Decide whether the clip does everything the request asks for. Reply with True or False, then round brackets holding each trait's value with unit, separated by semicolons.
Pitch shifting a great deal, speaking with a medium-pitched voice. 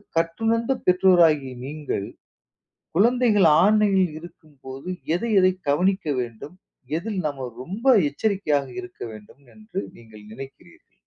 True (6.2 semitones; 175 Hz)